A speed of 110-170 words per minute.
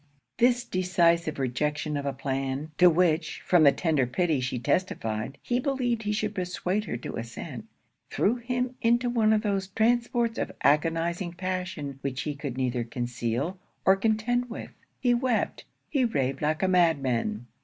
Yes: average, 160 wpm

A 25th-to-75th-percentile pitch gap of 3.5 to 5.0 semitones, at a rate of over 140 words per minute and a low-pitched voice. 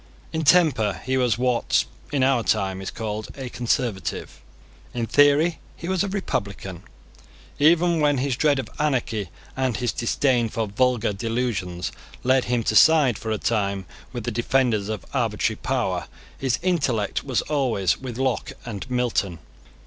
Yes: average, 4.1 semitones; average, 155 wpm; low, 125 Hz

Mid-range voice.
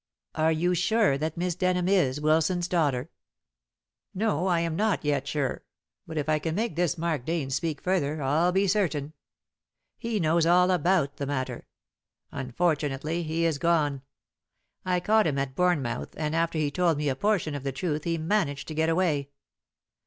Yes: medium, 160 Hz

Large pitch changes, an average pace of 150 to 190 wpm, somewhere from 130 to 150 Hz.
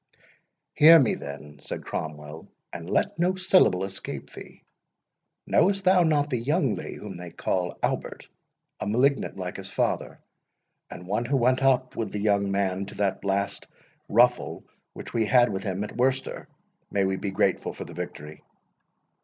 No: wide, 5.8 semitones; average, 160 wpm; low, 105 Hz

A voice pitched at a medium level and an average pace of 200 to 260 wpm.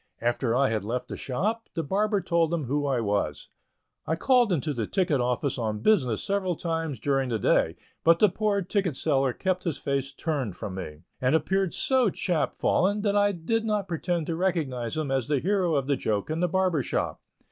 Yes: medium, 160 Hz; fast, 205 wpm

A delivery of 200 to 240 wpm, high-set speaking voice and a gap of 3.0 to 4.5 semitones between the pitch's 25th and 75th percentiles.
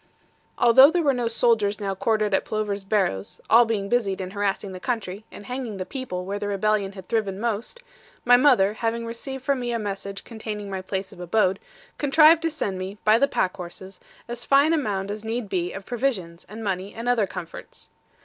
Yes: fast, 205 wpm; high, 215 Hz; average, 3.7 semitones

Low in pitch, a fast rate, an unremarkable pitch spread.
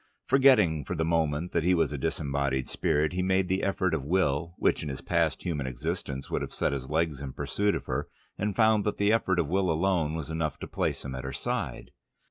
Yes: very low, 80 Hz; fast, 230 wpm; average, 4.7 semitones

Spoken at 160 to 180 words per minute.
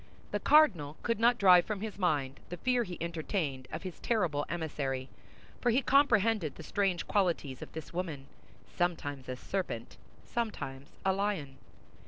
No: average, 150 wpm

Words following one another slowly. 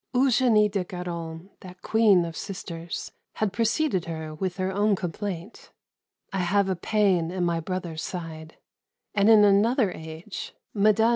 No: average, 145 wpm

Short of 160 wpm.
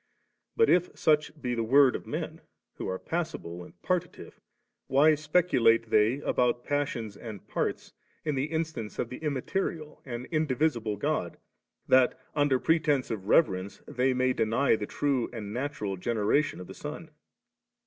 Yes: average, 150 wpm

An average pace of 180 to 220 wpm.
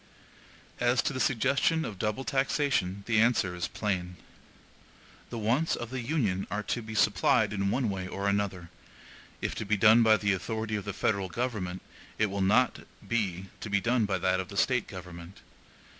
Yes: average, 185 wpm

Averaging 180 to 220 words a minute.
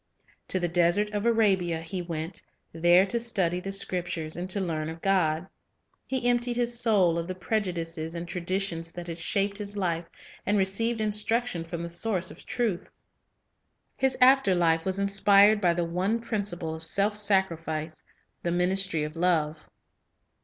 No: average, 160 wpm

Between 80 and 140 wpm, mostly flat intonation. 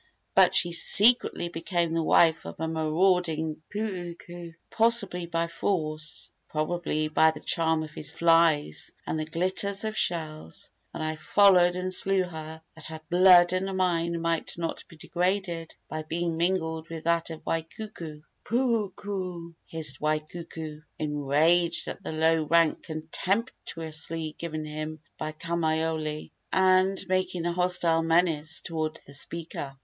Yes: slow, 135 wpm; narrow, 2.2 semitones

